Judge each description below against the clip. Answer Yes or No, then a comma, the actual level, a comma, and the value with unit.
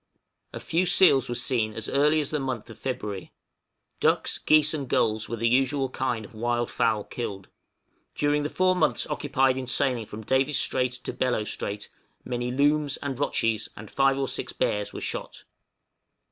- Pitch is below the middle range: Yes, low, 130 Hz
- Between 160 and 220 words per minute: Yes, average, 175 wpm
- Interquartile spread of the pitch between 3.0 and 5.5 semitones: Yes, average, 4.0 semitones